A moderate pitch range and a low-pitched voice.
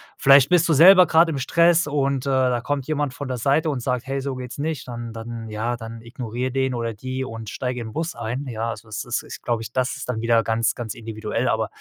Yes: average, 3.3 semitones; low, 125 Hz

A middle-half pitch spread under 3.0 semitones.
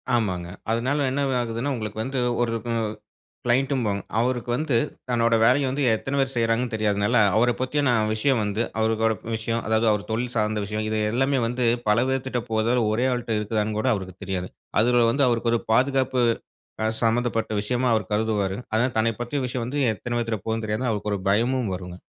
Yes: narrow, 2.6 semitones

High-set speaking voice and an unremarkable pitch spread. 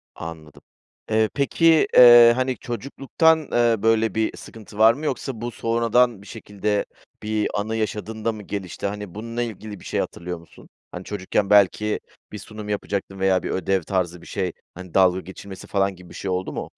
No: low, 105 Hz; average, 3.3 semitones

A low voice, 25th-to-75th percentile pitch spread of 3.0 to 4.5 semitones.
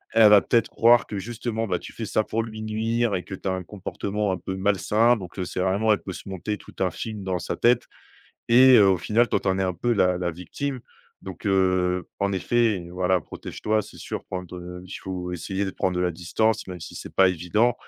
Yes: very low, 95 Hz; average, 3.4 semitones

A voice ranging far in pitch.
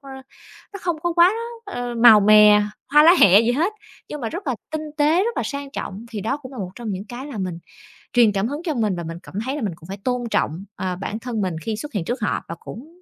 Yes: wide, 6.5 semitones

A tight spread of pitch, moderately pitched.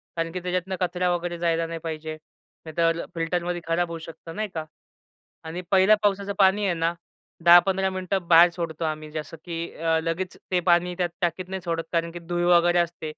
Yes: narrow, 1.6 semitones; medium, 170 Hz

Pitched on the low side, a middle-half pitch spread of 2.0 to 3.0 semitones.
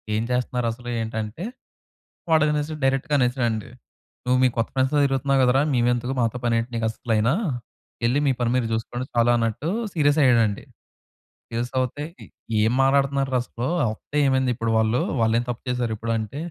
Yes: low, 125 Hz; average, 2.7 semitones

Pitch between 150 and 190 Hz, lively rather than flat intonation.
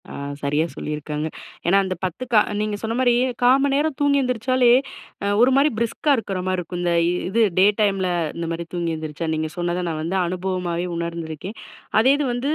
Yes: medium, 185 Hz; wide, 6.3 semitones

